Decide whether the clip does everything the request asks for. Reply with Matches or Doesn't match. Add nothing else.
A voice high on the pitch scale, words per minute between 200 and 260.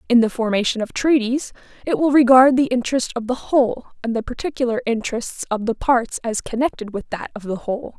Matches